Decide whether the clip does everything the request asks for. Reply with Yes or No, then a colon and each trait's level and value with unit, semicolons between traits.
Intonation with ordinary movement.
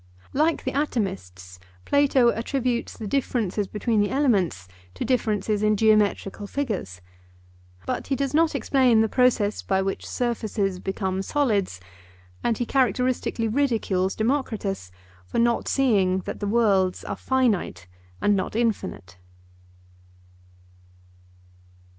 Yes: average, 4.6 semitones